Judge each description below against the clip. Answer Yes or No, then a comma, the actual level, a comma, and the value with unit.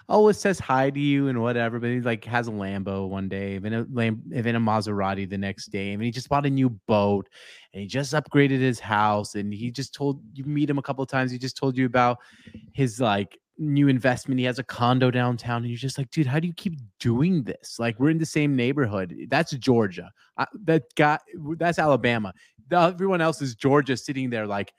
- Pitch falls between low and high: No, low, 125 Hz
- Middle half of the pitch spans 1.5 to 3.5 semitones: No, average, 4.5 semitones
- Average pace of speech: No, fast, 230 wpm